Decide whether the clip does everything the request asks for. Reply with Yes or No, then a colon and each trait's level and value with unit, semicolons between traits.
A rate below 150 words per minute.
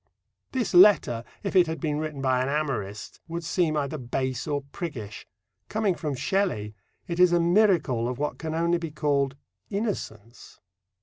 No: average, 165 wpm